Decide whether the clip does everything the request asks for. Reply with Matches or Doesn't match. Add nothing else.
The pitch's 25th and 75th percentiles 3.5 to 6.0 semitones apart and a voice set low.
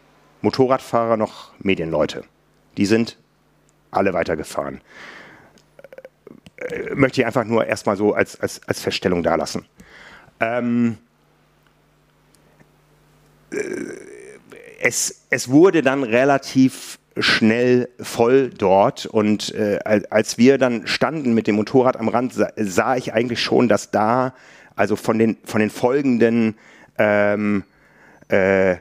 Matches